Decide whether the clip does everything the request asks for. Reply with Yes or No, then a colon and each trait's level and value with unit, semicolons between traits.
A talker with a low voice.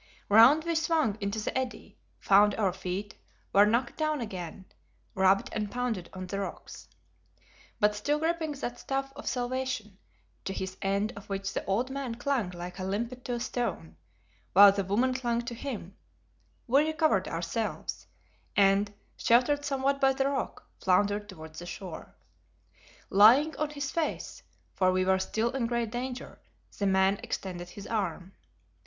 No: high, 215 Hz